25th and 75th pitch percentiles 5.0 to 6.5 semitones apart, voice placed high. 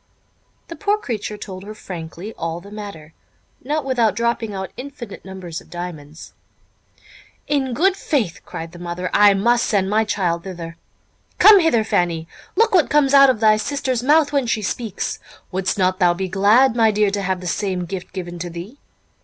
Yes: wide, 5.6 semitones; high, 205 Hz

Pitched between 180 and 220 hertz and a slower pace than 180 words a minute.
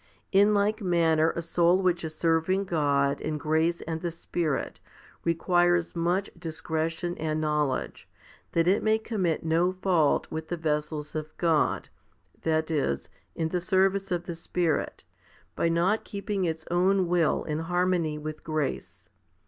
No: medium, 170 Hz; average, 150 wpm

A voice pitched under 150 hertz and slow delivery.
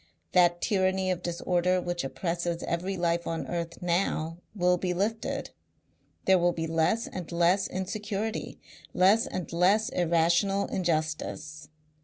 No: medium, 175 Hz; slow, 130 wpm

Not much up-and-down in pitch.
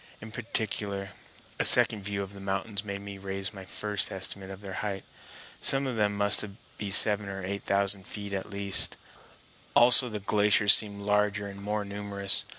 Yes: narrow, 1.1 semitones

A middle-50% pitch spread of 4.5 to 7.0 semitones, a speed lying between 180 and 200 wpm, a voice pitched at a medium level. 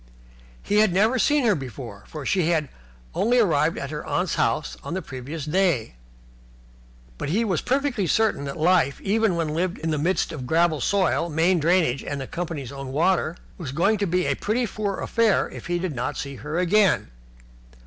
Yes: average, 4.9 semitones; average, 190 wpm; medium, 170 Hz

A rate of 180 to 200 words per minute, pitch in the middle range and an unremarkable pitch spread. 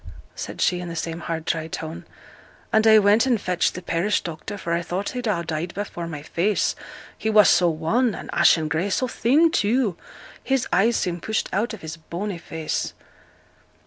Yes: average, 190 wpm; medium, 180 Hz; average, 4.6 semitones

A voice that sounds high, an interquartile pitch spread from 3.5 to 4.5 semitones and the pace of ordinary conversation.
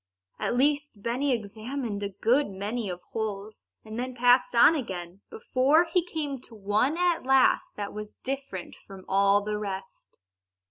No: high, 230 Hz; average, 5.1 semitones; average, 150 wpm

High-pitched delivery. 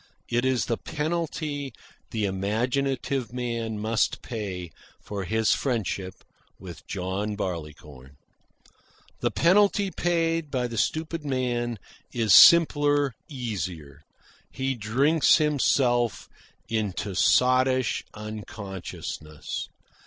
No: low, 120 Hz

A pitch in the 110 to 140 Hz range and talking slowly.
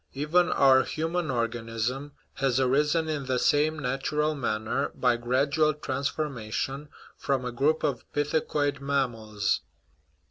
Yes: low, 135 Hz; slow, 115 wpm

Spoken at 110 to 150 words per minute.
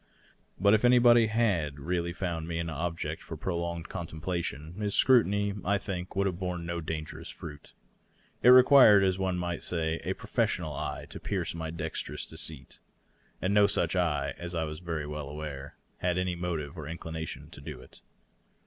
No: average, 175 wpm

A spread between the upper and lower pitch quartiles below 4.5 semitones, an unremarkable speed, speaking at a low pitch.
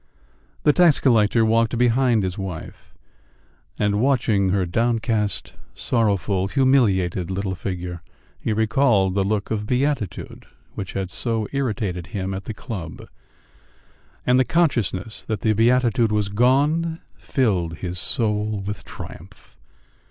No: average, 4.1 semitones; slow, 125 wpm; low, 105 Hz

